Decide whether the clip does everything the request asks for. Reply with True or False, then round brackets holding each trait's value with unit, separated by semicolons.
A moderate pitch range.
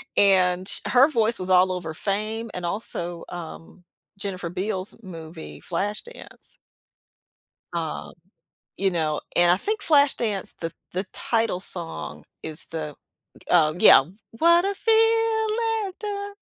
False (8.8 semitones)